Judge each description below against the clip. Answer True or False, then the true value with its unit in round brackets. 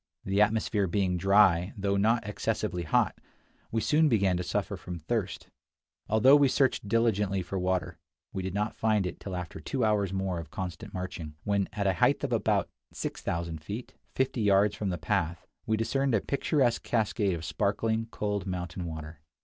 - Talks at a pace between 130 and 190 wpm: True (175 wpm)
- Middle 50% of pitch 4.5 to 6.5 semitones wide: False (3.4 semitones)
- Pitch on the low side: True (100 Hz)